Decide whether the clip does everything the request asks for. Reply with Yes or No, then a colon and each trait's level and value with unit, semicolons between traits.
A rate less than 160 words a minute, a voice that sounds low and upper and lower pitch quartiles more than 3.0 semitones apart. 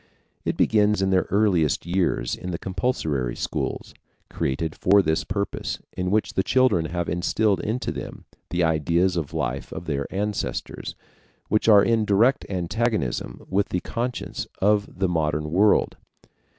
Yes: average, 150 wpm; very low, 95 Hz; average, 4.1 semitones